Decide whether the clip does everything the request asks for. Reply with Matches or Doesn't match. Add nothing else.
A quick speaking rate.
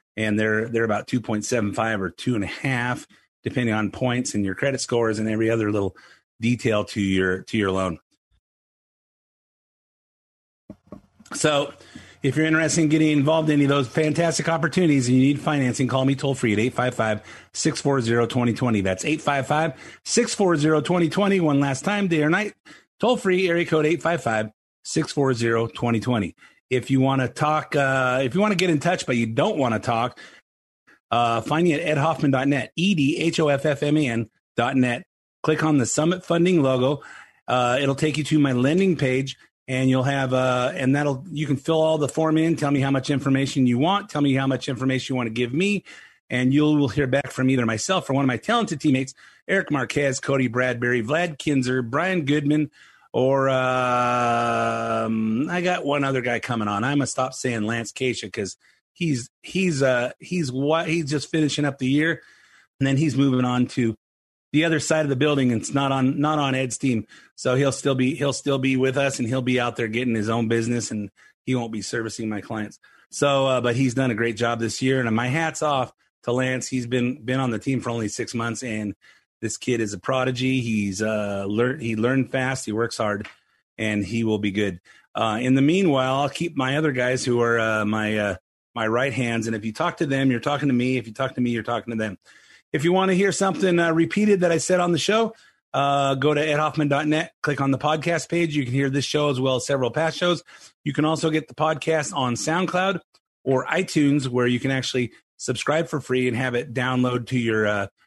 Matches